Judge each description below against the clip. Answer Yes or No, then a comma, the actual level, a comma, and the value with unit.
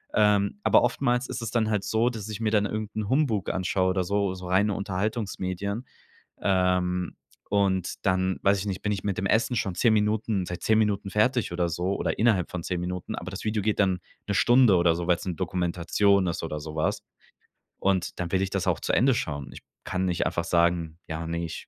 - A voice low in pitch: Yes, very low, 95 Hz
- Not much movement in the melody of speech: No, average, 3.0 semitones